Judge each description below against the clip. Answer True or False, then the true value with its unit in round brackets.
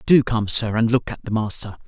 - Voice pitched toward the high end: False (115 Hz)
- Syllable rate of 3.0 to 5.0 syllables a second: False (5.3 syllables/s)